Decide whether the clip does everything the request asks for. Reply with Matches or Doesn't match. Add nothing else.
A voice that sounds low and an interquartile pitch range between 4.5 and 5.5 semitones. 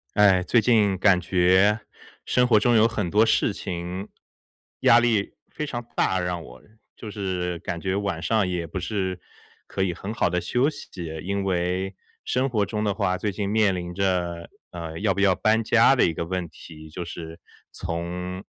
Doesn't match